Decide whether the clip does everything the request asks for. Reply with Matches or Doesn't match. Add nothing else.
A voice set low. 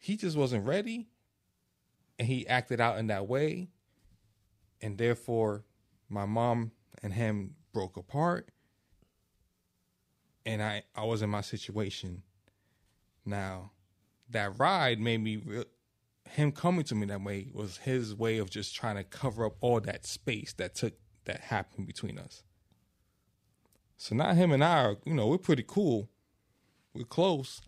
Matches